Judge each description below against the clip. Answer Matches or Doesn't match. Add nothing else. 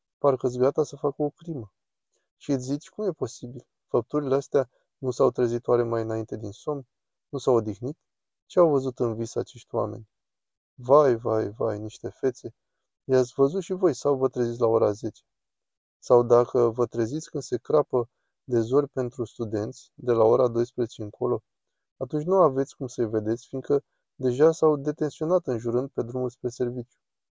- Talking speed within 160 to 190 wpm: Matches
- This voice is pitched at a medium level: Doesn't match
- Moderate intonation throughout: Matches